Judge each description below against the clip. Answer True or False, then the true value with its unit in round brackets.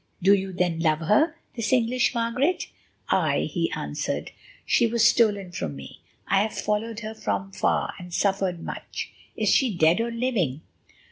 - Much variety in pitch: False (4.5 semitones)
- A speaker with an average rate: True (155 wpm)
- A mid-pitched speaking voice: False (210 Hz)